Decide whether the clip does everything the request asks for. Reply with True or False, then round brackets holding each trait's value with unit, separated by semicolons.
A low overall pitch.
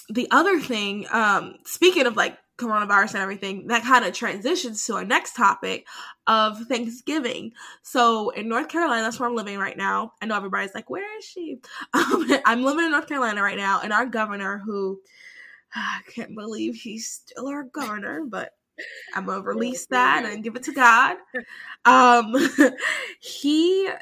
False (240 Hz)